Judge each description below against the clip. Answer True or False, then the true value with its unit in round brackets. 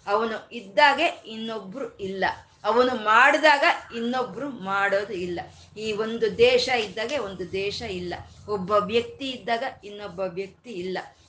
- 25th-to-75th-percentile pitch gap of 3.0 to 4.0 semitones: True (3.3 semitones)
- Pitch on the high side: True (215 Hz)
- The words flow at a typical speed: False (115 wpm)